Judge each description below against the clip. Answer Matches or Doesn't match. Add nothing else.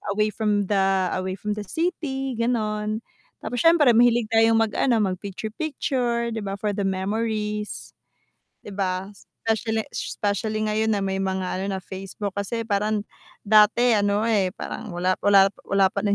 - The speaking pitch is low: Doesn't match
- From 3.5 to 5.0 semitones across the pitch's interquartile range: Doesn't match